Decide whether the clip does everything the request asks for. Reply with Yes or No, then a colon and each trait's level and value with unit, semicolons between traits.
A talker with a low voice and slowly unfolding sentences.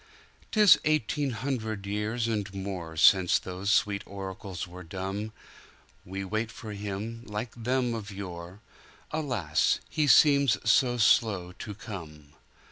Yes: low, 105 Hz; slow, 115 wpm